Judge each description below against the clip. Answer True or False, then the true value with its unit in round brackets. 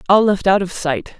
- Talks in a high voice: False (180 Hz)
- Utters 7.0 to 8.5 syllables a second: False (5.1 syllables/s)